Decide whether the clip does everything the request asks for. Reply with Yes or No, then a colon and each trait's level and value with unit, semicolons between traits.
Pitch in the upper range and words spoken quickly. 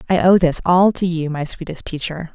No: medium, 170 Hz; fast, 230 wpm